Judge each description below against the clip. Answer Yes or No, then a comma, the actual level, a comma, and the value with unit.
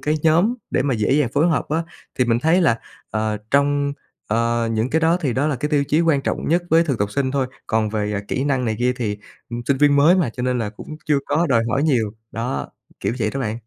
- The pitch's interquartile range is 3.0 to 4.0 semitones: No, average, 4.8 semitones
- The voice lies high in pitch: No, low, 135 Hz